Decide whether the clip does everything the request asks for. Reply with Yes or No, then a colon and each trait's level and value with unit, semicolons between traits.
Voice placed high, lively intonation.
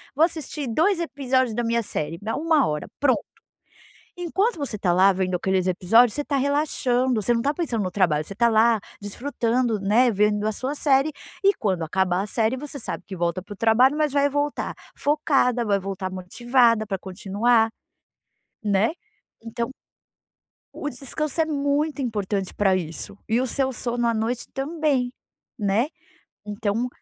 Yes: high, 235 Hz; wide, 5.7 semitones